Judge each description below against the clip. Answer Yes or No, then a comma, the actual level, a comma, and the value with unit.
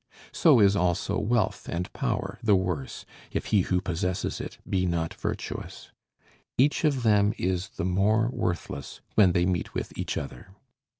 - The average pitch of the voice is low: Yes, very low, 95 Hz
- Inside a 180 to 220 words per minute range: No, average, 160 wpm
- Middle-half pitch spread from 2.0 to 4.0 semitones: Yes, average, 3.0 semitones